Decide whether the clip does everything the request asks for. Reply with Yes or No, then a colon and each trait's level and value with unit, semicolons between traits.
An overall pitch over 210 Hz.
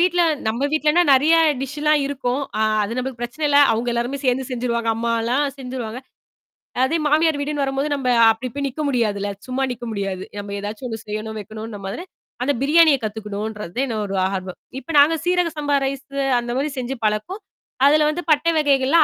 Yes: very high, 260 Hz